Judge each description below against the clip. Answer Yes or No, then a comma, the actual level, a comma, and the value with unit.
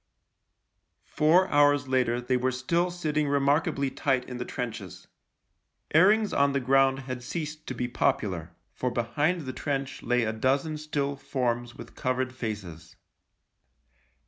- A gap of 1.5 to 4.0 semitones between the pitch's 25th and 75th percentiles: Yes, average, 3.2 semitones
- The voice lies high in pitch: No, low, 135 Hz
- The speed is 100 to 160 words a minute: Yes, average, 145 wpm